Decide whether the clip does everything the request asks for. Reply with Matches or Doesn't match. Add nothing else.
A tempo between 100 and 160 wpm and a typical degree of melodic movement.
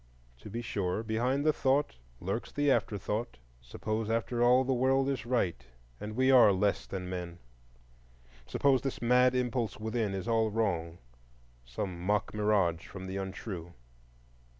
Matches